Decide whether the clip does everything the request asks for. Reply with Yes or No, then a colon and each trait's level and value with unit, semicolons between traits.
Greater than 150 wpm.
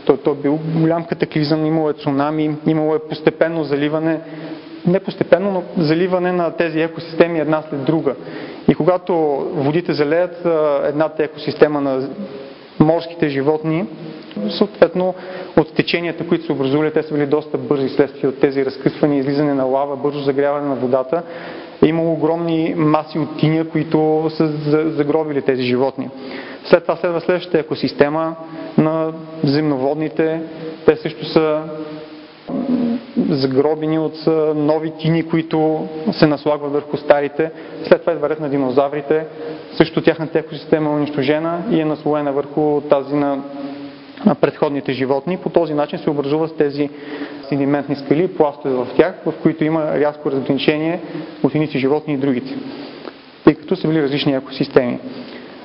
No: average, 140 wpm